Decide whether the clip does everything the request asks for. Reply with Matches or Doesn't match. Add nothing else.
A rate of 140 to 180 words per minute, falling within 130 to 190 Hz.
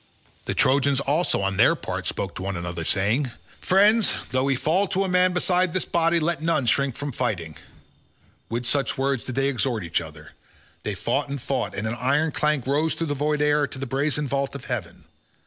Doesn't match